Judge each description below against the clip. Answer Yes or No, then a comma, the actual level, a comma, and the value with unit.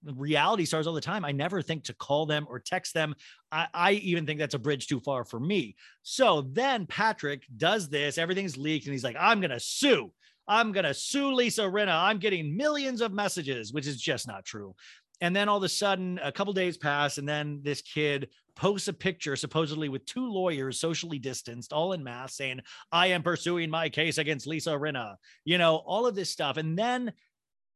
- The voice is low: No, medium, 160 Hz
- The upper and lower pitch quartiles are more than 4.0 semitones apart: Yes, average, 4.9 semitones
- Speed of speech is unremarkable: No, fast, 210 wpm